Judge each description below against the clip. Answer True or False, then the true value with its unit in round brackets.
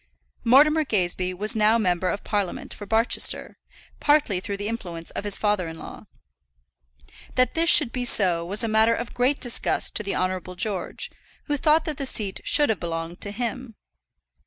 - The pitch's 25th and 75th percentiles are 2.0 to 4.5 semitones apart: False (5.1 semitones)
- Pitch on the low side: False (215 Hz)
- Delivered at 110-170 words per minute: False (180 wpm)